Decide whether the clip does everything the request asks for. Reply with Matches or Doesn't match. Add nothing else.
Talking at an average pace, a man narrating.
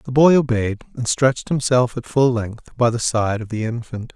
Doesn't match